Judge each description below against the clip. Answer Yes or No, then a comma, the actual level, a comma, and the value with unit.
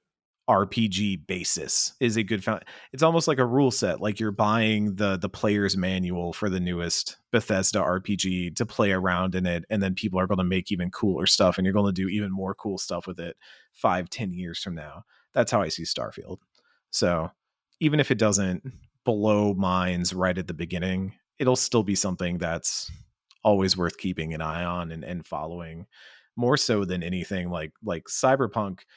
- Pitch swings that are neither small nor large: Yes, average, 3.0 semitones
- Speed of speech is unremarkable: Yes, average, 190 wpm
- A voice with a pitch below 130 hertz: Yes, very low, 95 Hz